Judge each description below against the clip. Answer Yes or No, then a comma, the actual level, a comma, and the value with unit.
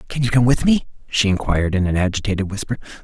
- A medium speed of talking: No, fast, 220 wpm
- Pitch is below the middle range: Yes, low, 110 Hz